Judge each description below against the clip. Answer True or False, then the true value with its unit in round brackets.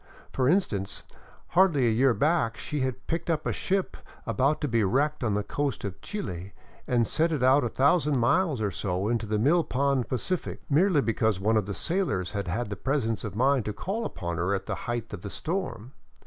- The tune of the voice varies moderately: False (6.2 semitones)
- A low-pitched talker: True (125 Hz)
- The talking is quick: True (210 wpm)